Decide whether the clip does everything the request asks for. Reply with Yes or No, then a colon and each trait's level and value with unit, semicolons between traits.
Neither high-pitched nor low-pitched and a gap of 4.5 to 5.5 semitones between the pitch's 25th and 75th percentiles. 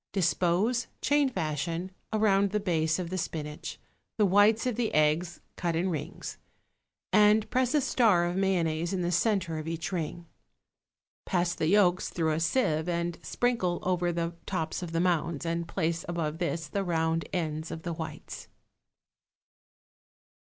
No: medium, 175 Hz; average, 3.1 semitones